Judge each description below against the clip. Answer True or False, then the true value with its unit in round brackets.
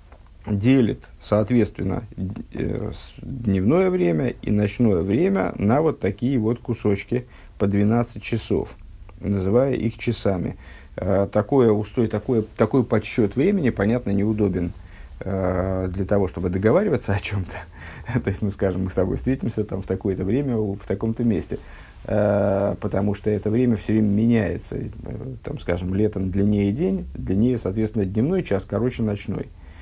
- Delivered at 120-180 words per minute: True (130 wpm)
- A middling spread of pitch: True (3.5 semitones)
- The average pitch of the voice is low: True (105 Hz)